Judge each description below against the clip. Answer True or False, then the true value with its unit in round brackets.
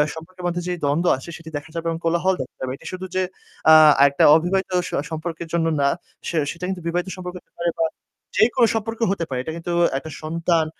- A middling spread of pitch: False (2.1 semitones)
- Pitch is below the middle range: False (170 Hz)